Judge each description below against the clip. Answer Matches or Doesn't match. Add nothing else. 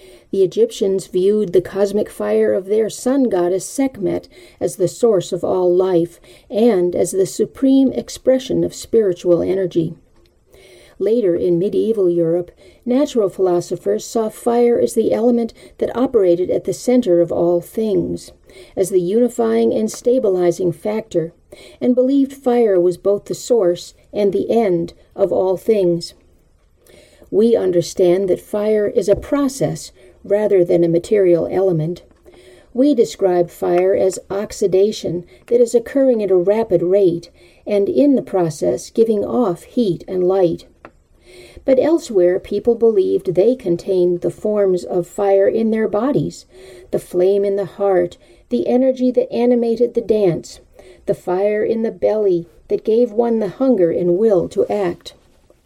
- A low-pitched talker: Doesn't match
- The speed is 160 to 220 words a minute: Doesn't match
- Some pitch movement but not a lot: Matches